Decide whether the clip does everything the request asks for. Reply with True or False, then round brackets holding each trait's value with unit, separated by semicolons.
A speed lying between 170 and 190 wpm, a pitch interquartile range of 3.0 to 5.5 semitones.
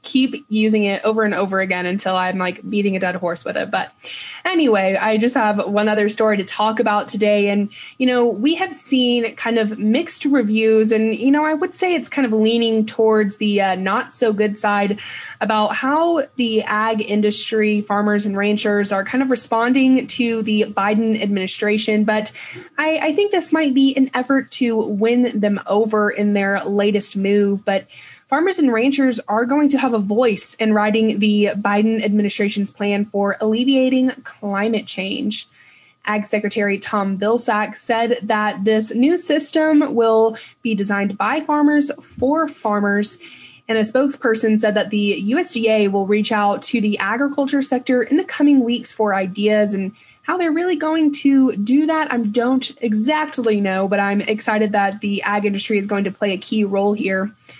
True (180 wpm; 4.0 semitones)